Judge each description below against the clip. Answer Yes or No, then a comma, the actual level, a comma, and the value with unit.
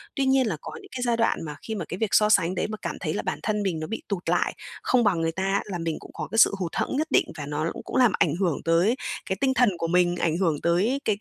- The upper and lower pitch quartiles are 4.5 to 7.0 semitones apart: Yes, average, 5.1 semitones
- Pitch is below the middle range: No, high, 190 Hz